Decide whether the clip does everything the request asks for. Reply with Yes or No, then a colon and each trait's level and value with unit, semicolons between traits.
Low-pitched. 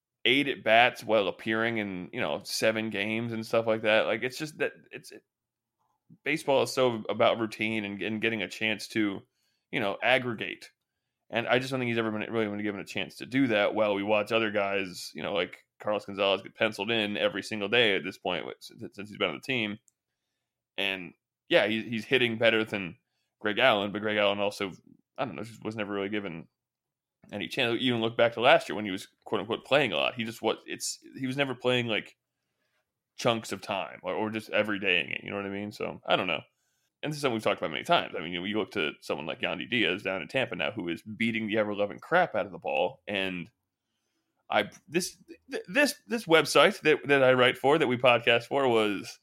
Yes: low, 110 Hz